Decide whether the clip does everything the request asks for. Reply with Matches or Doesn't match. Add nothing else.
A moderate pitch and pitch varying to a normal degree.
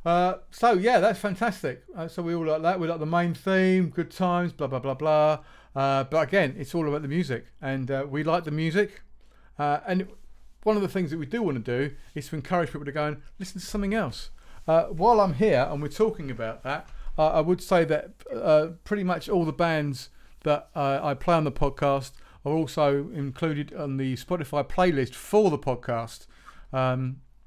Matches